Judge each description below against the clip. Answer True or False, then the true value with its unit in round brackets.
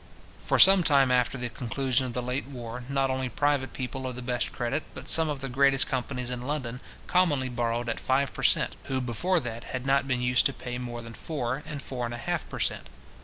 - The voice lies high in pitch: False (130 Hz)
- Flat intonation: True (2.1 semitones)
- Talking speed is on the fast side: True (230 wpm)